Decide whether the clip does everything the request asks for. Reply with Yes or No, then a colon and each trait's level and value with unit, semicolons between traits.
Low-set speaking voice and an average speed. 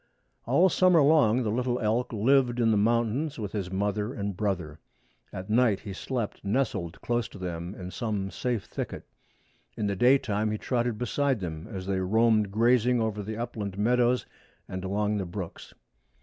Yes: low, 110 Hz; average, 170 wpm